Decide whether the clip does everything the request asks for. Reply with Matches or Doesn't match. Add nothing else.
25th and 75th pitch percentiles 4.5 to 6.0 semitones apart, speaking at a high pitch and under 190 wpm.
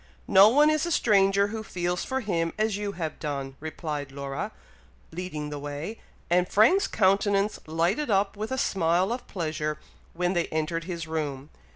Doesn't match